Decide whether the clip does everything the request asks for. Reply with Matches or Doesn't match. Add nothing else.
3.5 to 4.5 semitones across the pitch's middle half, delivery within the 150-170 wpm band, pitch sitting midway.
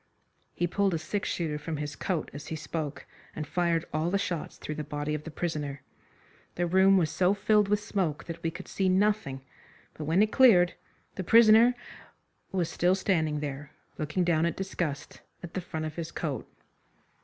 Doesn't match